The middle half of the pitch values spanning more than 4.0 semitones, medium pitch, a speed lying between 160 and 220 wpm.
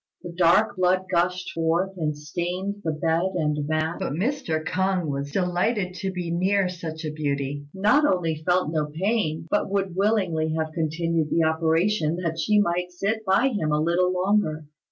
No: average, 3.2 semitones; medium, 175 Hz; average, 175 wpm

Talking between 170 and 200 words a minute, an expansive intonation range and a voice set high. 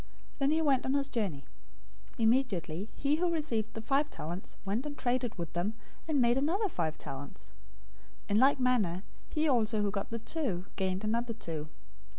Yes: average, 180 wpm; wide, 6.3 semitones; high, 230 Hz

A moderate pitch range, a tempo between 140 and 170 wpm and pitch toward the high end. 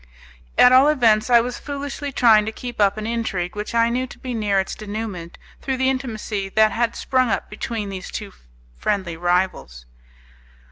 No: average, 3.9 semitones; average, 180 wpm; high, 220 Hz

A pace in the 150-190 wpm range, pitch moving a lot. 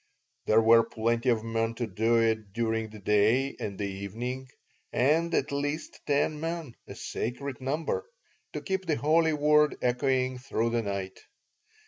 No: average, 155 wpm; average, 4.5 semitones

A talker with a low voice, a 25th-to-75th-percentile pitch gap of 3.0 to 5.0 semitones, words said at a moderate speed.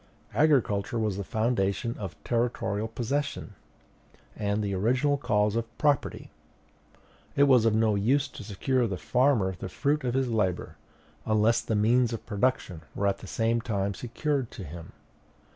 Yes: low, 115 Hz; average, 4.0 semitones; average, 160 wpm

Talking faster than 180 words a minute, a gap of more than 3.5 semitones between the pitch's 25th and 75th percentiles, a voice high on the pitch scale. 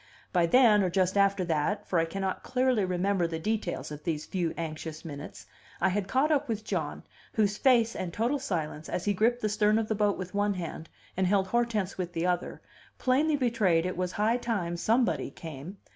Yes: fast, 205 wpm; average, 4.4 semitones; high, 195 Hz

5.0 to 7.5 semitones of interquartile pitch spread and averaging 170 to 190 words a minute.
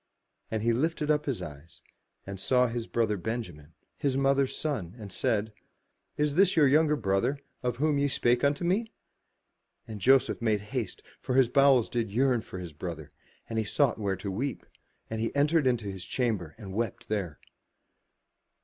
Yes: wide, 5.4 semitones; average, 175 wpm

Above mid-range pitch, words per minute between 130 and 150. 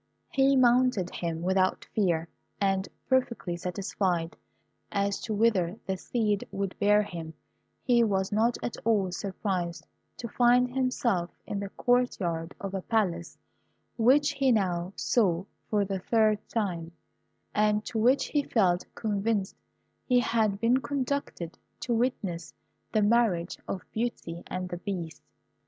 Yes: high, 205 Hz; average, 140 wpm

